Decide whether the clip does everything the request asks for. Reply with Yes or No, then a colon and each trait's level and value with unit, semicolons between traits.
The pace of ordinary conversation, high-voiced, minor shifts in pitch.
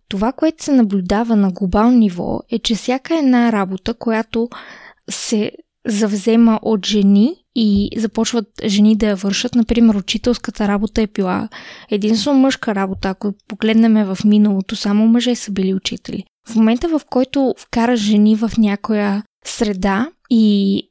Yes: average, 145 wpm; high, 220 Hz; narrow, 2.2 semitones